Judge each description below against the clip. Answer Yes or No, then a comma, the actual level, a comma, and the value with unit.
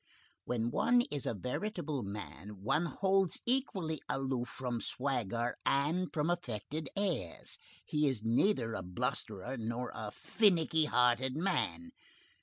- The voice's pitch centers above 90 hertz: Yes, low, 135 Hz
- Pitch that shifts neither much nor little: No, wide, 6.6 semitones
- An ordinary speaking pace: No, slow, 125 wpm